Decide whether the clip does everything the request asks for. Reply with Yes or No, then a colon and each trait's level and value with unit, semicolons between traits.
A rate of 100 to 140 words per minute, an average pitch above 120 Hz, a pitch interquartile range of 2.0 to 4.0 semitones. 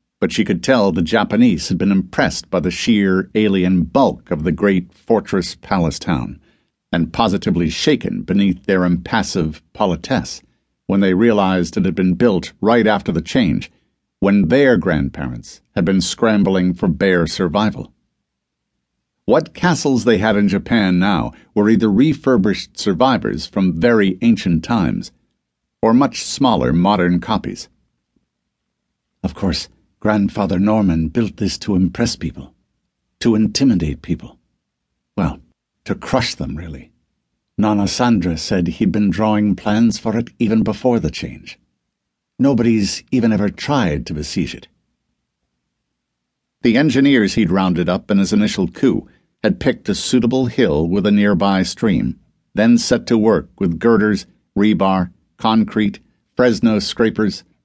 No: slow, 135 wpm; low, 100 Hz; average, 3.7 semitones